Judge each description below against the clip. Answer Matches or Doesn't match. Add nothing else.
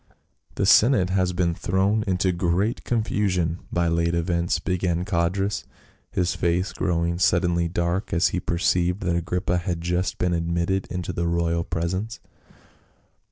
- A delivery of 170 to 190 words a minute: Doesn't match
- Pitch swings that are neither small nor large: Doesn't match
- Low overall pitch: Matches